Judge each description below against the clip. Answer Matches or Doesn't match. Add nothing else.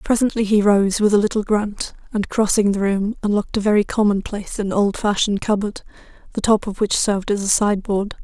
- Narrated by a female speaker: Matches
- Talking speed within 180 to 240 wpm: Matches